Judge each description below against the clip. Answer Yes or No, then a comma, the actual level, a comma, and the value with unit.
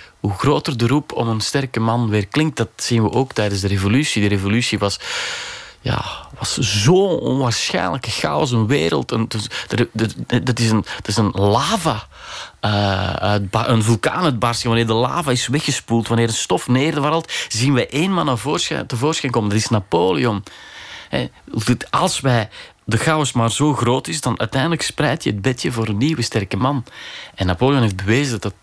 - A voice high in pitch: No, low, 115 Hz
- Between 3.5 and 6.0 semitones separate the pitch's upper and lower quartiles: Yes, average, 4.2 semitones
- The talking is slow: No, average, 170 wpm